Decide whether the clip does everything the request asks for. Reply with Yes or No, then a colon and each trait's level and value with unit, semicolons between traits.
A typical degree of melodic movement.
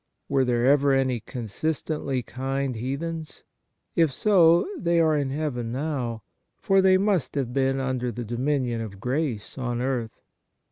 Yes: average, 4.2 semitones